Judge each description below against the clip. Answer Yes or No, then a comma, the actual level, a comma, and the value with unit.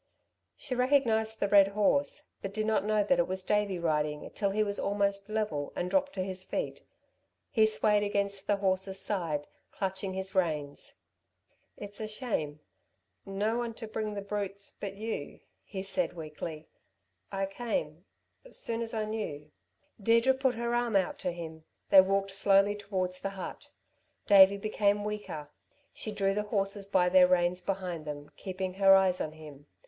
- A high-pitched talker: Yes, high, 195 Hz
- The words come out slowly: No, average, 165 wpm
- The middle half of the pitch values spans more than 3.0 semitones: No, narrow, 2.6 semitones